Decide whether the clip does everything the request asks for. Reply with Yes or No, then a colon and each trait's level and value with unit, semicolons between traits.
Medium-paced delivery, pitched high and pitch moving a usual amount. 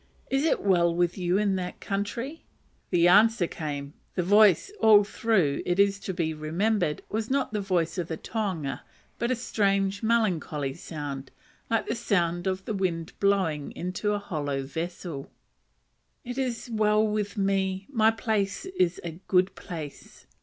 Yes: average, 160 wpm; high, 195 Hz; average, 4.1 semitones